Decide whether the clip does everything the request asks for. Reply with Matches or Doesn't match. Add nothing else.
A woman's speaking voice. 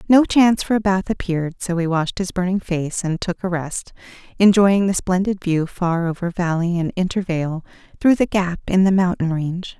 Matches